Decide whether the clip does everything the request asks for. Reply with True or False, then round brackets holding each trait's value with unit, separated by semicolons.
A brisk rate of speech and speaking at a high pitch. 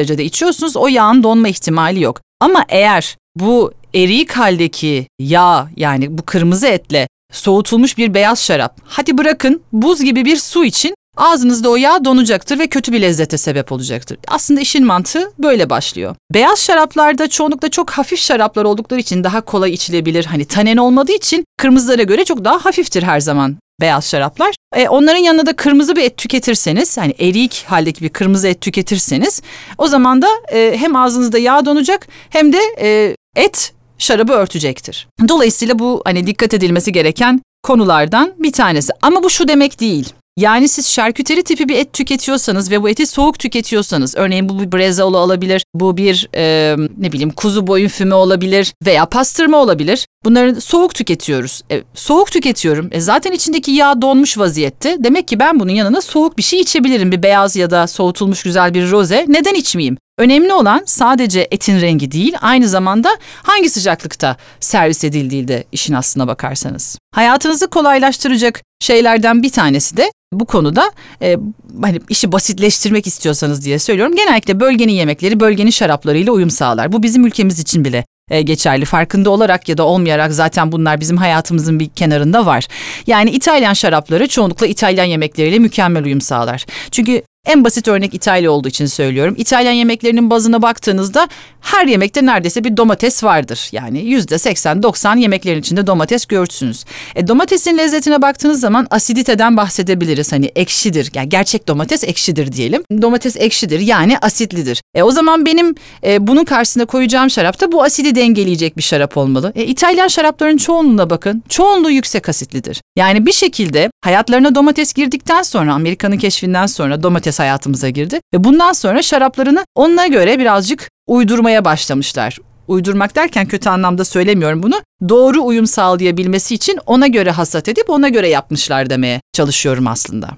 True (160 wpm; 215 Hz)